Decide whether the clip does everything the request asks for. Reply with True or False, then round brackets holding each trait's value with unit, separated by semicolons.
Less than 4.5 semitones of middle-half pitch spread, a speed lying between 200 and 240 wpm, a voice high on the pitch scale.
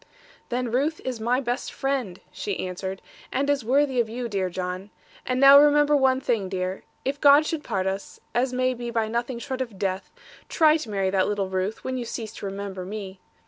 False (5.3 semitones; 205 wpm; 235 Hz)